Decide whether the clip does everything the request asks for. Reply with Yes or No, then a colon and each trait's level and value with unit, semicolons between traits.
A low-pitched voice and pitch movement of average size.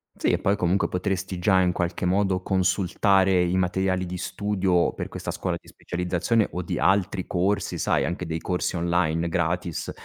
No: very low, 90 Hz; narrow, 1.5 semitones